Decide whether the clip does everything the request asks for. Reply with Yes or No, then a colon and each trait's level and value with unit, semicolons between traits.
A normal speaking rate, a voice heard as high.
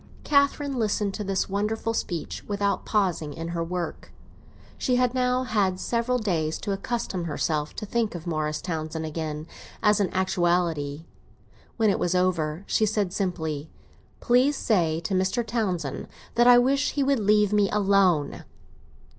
Yes: average, 155 wpm; high, 195 Hz